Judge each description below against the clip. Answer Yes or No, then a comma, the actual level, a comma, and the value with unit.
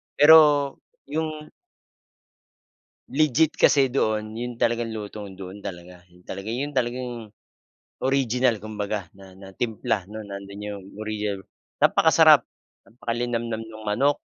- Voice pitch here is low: Yes, low, 110 Hz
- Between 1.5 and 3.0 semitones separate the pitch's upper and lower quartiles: No, average, 3.5 semitones